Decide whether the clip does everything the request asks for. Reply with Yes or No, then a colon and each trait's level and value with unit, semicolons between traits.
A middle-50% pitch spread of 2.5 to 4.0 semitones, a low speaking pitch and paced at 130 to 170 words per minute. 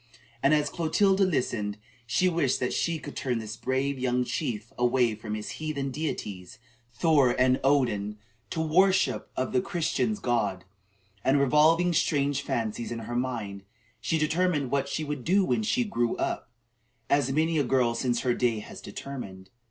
No: average, 4.9 semitones; low, 130 Hz; average, 165 wpm